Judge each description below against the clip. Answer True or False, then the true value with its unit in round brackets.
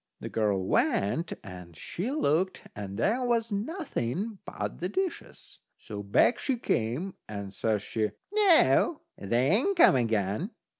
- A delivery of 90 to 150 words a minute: True (140 wpm)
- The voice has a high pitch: False (150 Hz)